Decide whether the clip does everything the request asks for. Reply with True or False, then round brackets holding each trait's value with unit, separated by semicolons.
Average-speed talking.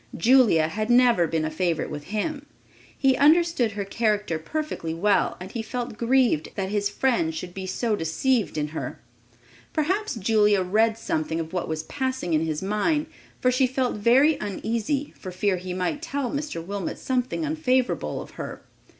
True (170 wpm)